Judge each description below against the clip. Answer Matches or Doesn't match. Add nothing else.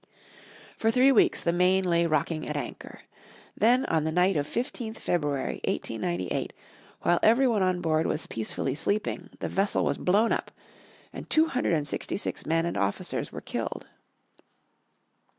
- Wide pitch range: Matches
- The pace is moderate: Matches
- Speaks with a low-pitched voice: Doesn't match